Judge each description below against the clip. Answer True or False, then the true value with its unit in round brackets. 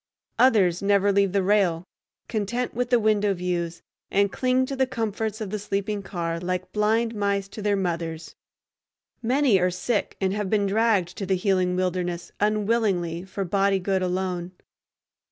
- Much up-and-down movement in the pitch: False (2.8 semitones)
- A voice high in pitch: True (200 Hz)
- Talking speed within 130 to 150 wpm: False (160 wpm)